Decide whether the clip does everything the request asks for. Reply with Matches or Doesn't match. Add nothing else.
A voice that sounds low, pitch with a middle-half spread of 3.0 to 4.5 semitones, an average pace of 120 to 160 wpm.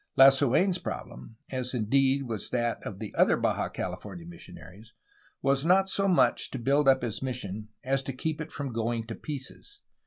Doesn't match